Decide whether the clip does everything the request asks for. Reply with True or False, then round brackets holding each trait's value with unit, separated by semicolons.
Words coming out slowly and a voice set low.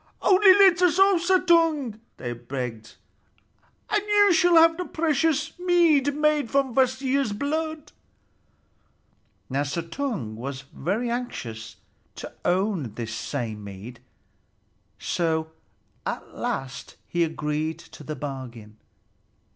False (110 wpm; 230 Hz)